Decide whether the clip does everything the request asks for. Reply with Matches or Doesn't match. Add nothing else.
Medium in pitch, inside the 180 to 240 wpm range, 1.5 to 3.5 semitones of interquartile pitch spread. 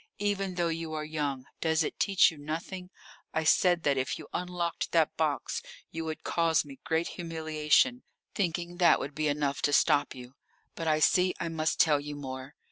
Matches